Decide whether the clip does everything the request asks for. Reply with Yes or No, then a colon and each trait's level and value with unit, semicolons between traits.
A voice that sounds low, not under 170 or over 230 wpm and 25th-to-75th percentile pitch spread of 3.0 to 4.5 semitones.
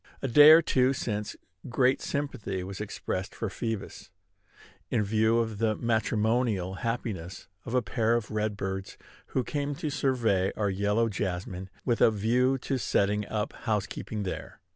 No: low, 110 Hz; average, 155 wpm; average, 3.4 semitones